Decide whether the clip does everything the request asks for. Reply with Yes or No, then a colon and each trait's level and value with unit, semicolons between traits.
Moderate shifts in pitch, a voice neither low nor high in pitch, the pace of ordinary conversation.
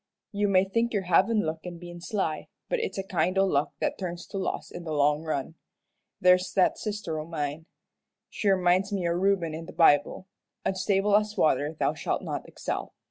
Yes: average, 3.4 semitones; medium, 180 Hz; average, 195 wpm